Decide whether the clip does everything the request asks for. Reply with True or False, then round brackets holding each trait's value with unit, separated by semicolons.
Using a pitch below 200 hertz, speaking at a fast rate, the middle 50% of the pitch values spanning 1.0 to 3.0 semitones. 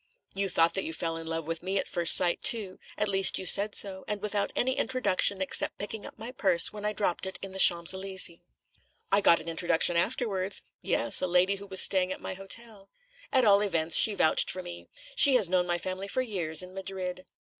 True (190 Hz; 220 wpm; 2.6 semitones)